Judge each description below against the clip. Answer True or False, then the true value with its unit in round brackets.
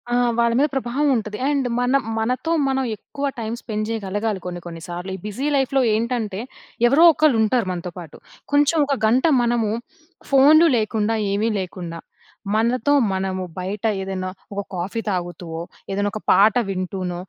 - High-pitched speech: True (215 Hz)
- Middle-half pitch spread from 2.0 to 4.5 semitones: False (5.1 semitones)